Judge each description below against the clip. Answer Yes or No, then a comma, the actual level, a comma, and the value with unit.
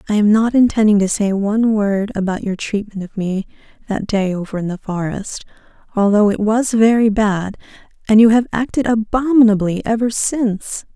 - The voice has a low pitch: No, high, 210 Hz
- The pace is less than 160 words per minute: No, average, 170 wpm